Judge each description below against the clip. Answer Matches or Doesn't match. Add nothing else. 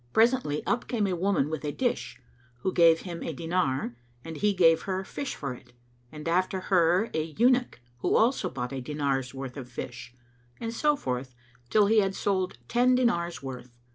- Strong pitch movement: Matches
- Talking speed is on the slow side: Doesn't match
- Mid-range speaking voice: Matches